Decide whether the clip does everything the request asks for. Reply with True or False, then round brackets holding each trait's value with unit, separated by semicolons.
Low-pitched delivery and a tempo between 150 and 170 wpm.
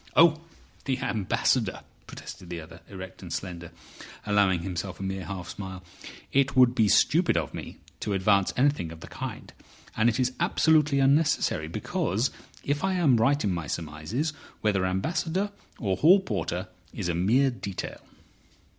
True (105 Hz; 155 wpm)